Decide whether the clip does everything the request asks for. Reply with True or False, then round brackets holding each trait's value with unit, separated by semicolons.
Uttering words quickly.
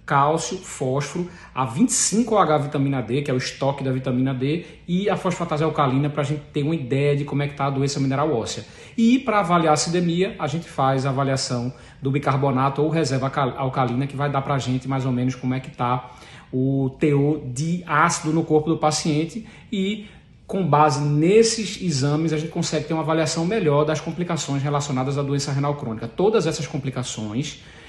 True (195 wpm)